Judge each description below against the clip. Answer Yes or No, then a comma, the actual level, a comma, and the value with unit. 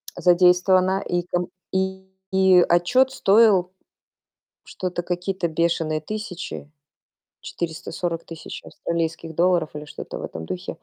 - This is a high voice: No, medium, 175 Hz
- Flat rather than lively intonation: Yes, narrow, 2.2 semitones